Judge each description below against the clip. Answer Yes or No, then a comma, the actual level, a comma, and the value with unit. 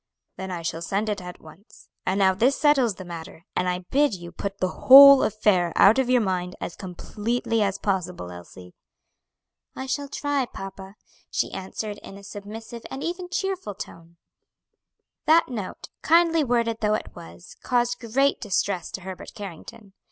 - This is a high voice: Yes, high, 205 Hz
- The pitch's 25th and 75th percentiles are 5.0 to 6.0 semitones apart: Yes, average, 5.3 semitones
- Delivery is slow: No, average, 165 wpm